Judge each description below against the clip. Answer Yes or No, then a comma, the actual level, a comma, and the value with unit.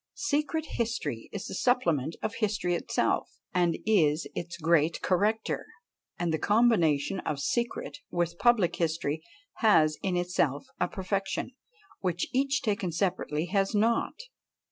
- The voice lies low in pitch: No, medium, 180 Hz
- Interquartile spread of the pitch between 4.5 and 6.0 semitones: Yes, average, 5.0 semitones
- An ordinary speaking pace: No, slow, 130 wpm